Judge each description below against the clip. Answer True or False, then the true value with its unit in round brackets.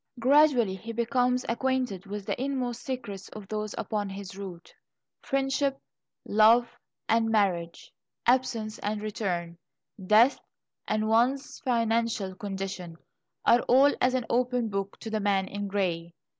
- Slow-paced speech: True (130 wpm)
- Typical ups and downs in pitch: True (4.0 semitones)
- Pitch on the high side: True (220 Hz)